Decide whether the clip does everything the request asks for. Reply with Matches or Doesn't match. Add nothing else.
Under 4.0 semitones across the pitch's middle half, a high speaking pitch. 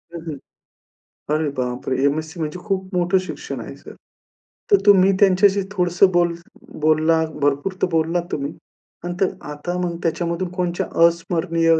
Doesn't match